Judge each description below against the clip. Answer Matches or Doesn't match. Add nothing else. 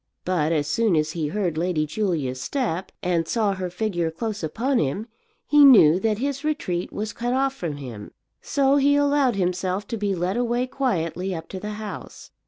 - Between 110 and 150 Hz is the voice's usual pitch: Doesn't match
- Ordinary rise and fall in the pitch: Doesn't match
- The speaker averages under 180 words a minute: Doesn't match